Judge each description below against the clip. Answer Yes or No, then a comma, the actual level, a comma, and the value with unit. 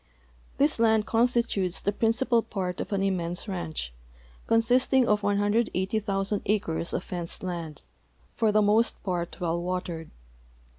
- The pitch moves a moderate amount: Yes, average, 4.1 semitones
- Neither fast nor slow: No, slow, 130 wpm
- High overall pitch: Yes, high, 200 Hz